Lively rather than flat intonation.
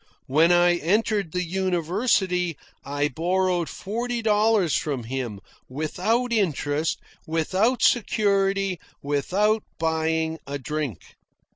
No: average, 4.7 semitones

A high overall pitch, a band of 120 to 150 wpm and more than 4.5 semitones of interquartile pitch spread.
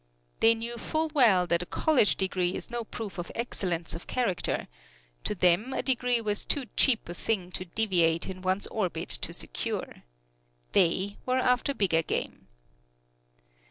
No: high, 205 Hz; average, 160 wpm; average, 5.1 semitones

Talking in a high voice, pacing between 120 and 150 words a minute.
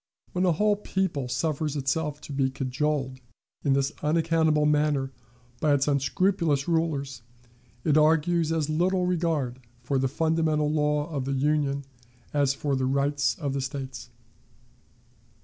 No: medium, 150 Hz; average, 140 wpm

